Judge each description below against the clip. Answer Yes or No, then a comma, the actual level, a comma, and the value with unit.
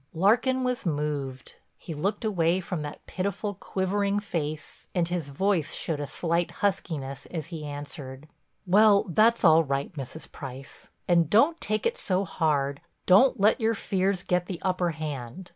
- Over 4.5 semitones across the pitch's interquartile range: Yes, average, 5.2 semitones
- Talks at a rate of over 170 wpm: No, average, 155 wpm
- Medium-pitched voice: Yes, medium, 175 Hz